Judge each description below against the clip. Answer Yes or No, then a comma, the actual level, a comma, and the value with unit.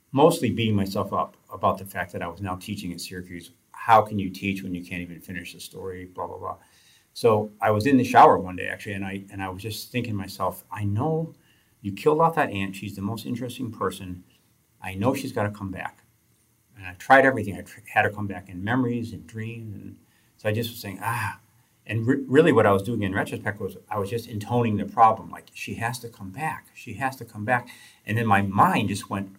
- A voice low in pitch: Yes, low, 105 Hz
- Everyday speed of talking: No, fast, 240 wpm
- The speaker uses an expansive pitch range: No, average, 3.2 semitones